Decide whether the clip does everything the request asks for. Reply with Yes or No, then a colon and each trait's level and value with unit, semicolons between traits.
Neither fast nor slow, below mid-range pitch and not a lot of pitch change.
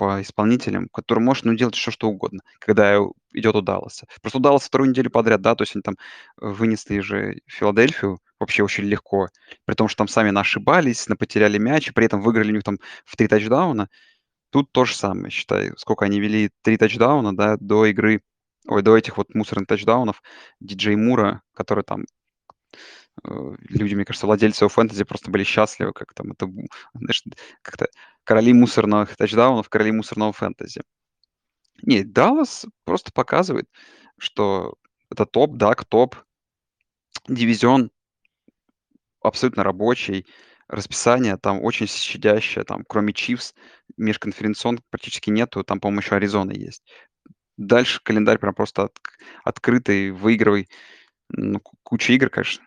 Yes: average, 140 wpm; low, 110 Hz; narrow, 2.3 semitones